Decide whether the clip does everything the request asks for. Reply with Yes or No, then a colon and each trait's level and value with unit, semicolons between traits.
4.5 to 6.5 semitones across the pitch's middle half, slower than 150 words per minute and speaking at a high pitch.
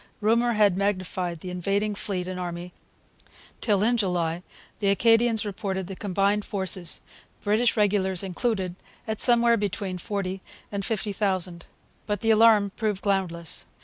No: narrow, 2.6 semitones; average, 140 wpm; high, 200 Hz